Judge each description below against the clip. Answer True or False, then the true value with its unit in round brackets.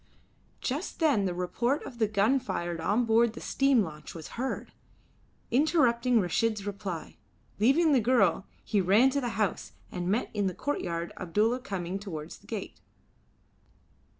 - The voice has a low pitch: False (215 Hz)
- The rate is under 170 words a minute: True (150 wpm)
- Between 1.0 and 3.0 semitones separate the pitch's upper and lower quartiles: False (5.3 semitones)